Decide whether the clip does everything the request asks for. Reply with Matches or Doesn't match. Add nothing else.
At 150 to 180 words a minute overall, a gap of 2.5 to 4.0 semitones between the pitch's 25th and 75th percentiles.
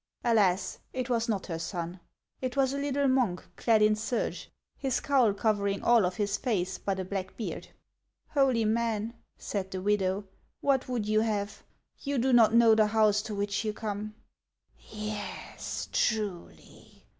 Matches